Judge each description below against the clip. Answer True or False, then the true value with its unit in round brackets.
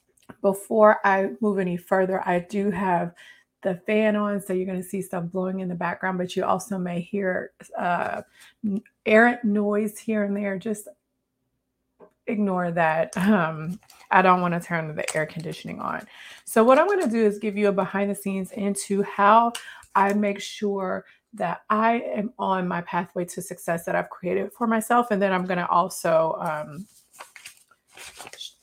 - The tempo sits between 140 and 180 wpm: True (170 wpm)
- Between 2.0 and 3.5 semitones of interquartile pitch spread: True (2.6 semitones)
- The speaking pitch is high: True (195 Hz)